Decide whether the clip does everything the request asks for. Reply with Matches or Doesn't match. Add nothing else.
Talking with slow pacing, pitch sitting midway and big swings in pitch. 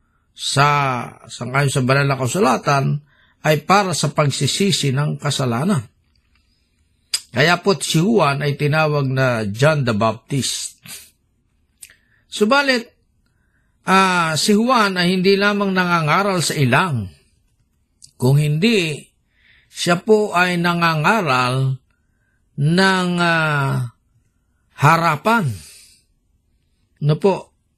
Matches